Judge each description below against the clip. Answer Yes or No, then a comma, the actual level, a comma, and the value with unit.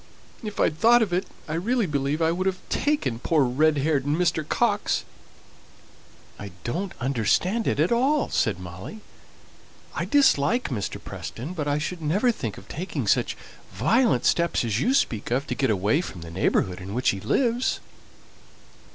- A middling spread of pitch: No, wide, 9.0 semitones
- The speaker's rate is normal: Yes, average, 170 wpm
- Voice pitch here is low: No, medium, 155 Hz